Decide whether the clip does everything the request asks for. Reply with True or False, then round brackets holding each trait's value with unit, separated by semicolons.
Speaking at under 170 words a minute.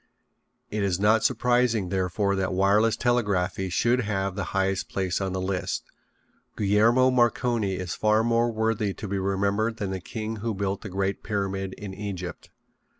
True (160 wpm)